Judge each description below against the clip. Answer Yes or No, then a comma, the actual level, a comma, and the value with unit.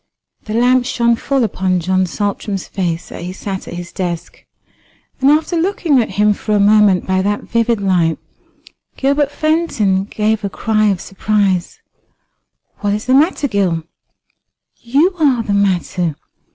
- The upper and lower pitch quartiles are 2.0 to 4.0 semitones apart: No, average, 4.7 semitones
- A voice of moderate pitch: No, high, 210 Hz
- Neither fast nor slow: Yes, average, 150 wpm